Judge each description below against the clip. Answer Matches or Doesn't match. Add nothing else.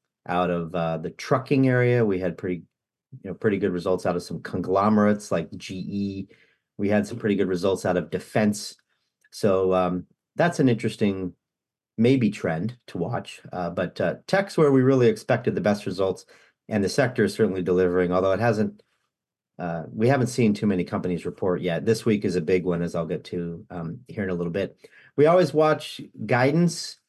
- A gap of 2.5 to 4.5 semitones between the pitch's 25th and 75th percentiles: Doesn't match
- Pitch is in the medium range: Doesn't match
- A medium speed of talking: Matches